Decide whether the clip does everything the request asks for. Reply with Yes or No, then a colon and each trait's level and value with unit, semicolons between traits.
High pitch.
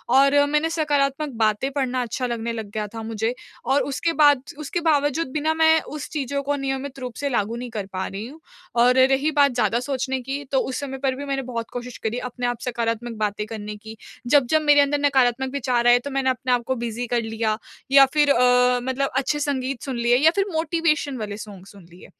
Yes: very high, 260 Hz